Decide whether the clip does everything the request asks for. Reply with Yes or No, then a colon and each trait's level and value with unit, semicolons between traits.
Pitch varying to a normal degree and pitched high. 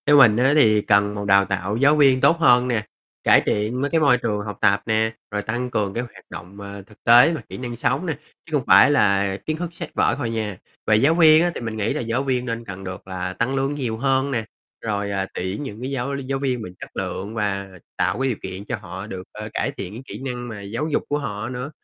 No: average, 4.8 semitones; low, 115 Hz